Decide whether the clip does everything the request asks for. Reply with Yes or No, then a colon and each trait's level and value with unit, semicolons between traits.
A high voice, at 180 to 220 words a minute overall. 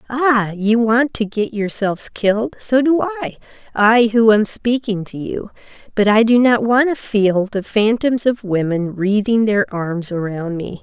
No: high, 215 Hz; average, 170 wpm